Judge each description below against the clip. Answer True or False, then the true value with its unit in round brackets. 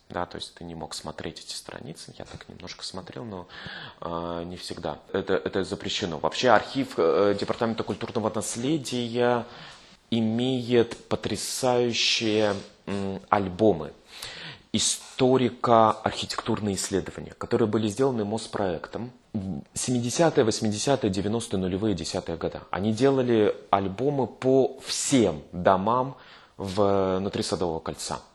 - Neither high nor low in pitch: False (110 Hz)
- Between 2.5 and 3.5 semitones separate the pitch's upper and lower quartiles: False (4.1 semitones)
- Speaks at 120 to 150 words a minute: False (110 wpm)